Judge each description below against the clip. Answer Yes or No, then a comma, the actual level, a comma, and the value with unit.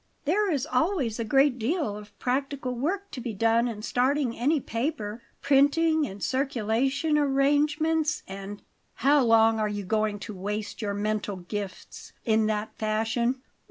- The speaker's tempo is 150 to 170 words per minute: Yes, average, 155 wpm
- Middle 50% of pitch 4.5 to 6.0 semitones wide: Yes, average, 5.1 semitones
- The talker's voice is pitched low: No, high, 240 Hz